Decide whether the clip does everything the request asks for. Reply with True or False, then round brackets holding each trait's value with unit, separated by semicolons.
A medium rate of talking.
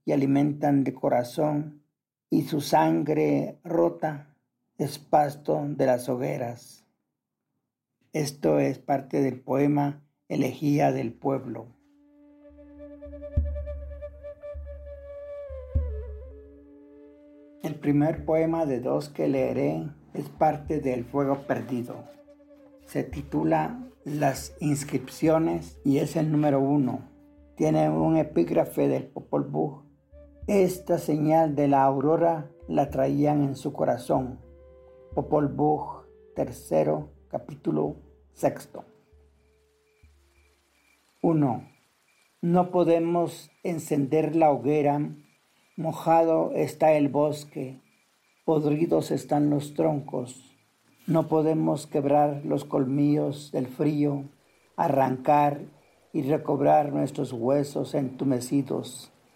False (90 wpm)